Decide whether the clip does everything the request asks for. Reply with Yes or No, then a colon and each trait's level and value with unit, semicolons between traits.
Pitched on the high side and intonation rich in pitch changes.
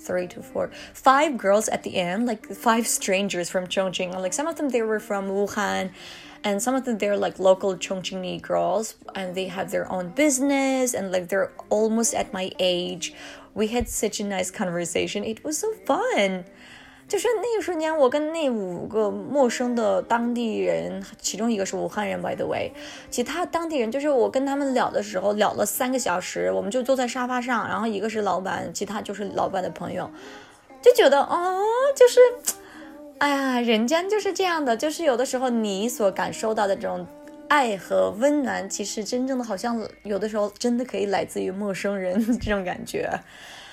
Yes: high, 220 Hz; wide, 5.9 semitones